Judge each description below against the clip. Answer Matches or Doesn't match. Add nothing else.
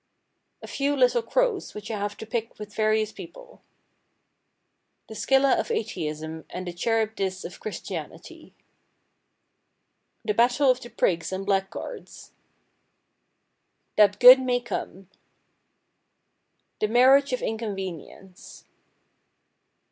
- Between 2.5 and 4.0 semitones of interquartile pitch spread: Doesn't match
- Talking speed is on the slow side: Matches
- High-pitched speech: Matches